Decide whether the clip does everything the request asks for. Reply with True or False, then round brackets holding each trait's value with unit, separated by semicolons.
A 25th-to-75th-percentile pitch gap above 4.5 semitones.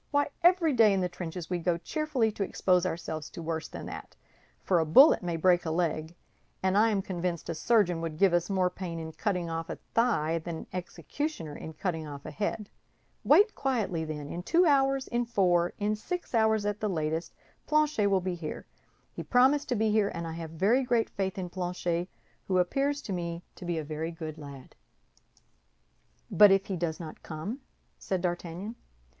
True (4.9 semitones)